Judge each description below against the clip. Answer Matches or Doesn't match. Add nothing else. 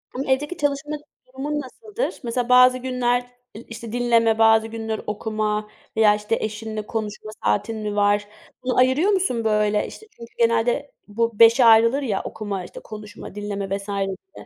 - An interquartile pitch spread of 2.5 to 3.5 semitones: Matches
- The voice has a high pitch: Matches